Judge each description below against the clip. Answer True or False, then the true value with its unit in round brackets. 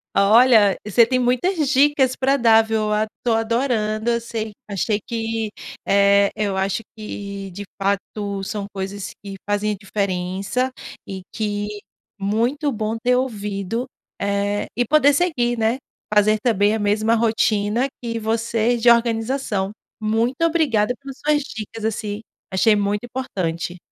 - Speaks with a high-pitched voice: True (220 Hz)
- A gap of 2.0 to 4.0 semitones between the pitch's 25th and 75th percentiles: True (3.0 semitones)